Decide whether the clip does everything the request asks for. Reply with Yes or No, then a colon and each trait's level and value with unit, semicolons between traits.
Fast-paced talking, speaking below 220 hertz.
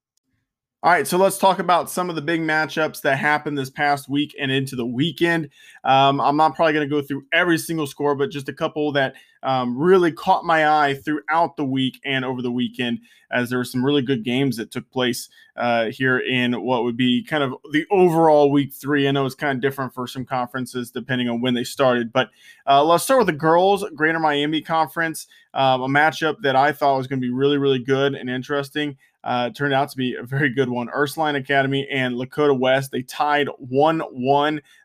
Yes: fast, 220 wpm; medium, 140 Hz